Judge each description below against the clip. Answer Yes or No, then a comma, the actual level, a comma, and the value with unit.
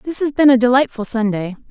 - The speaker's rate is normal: No, fast, 210 wpm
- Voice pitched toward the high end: Yes, high, 245 Hz